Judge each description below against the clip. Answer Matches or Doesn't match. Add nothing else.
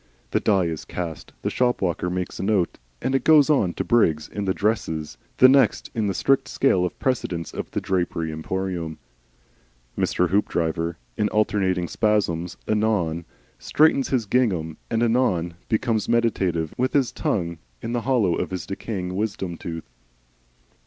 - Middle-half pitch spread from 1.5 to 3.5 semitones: Doesn't match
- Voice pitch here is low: Matches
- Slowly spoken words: Doesn't match